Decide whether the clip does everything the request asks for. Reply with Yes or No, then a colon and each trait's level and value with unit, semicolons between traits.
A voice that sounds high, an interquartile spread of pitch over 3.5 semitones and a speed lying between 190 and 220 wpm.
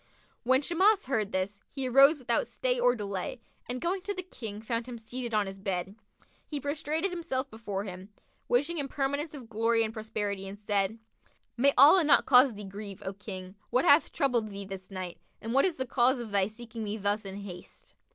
Yes: high, 230 Hz; average, 5.2 semitones; average, 200 wpm